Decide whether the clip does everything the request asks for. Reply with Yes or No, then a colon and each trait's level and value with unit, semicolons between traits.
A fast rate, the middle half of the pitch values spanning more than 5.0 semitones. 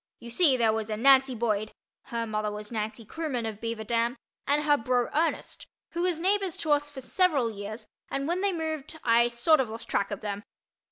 Yes: fast, 210 wpm; wide, 5.6 semitones